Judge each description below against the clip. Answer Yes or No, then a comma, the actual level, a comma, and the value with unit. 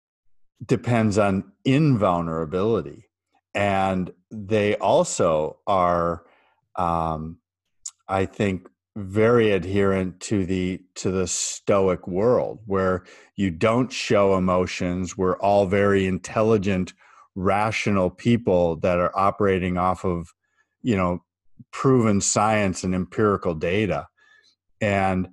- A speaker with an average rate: No, slow, 100 wpm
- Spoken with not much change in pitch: Yes, narrow, 2.3 semitones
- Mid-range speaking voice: No, very low, 95 Hz